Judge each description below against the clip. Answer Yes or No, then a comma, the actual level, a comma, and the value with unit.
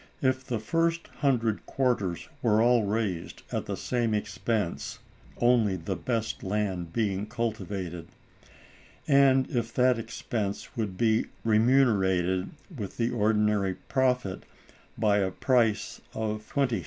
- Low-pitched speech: Yes, low, 110 Hz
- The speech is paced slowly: Yes, slow, 120 wpm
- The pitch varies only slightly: No, average, 3.7 semitones